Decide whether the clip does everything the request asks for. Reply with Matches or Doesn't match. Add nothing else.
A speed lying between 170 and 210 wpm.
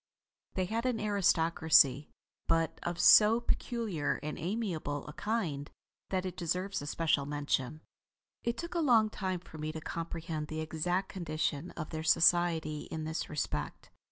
Doesn't match